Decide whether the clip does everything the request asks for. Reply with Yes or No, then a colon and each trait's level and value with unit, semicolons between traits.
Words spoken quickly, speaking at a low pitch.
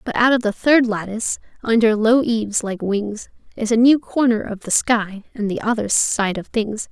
No: fast, 210 wpm; high, 225 Hz